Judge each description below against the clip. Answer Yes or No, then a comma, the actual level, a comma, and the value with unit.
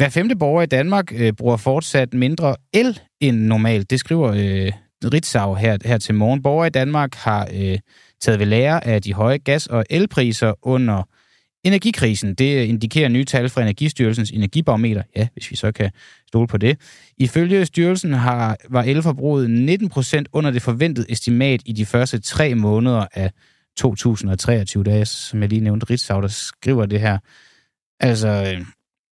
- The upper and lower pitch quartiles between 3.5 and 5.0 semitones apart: Yes, average, 4.6 semitones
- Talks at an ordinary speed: Yes, average, 170 wpm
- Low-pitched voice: Yes, low, 120 Hz